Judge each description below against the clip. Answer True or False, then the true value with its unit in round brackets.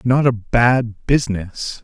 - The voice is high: False (115 Hz)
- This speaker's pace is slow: True (130 wpm)